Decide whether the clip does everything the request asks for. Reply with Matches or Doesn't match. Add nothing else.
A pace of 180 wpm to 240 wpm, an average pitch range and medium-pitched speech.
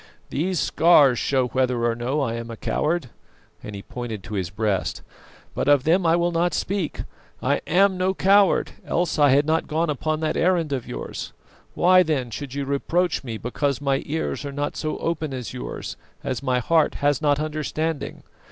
Matches